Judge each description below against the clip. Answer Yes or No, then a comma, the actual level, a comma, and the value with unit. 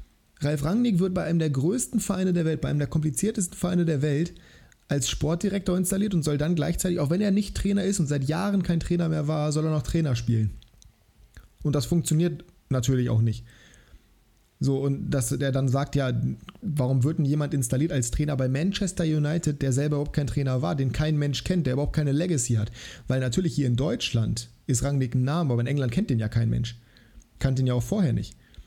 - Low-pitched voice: No, medium, 150 Hz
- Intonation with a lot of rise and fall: No, average, 4.6 semitones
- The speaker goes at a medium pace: No, fast, 215 wpm